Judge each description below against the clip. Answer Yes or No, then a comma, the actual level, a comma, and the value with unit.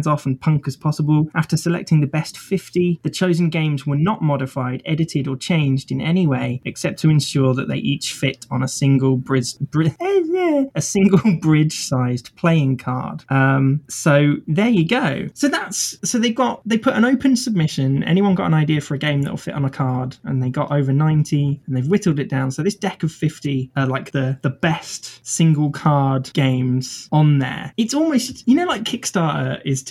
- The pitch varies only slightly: No, average, 4.4 semitones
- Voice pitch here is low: No, medium, 150 Hz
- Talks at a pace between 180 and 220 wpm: Yes, average, 200 wpm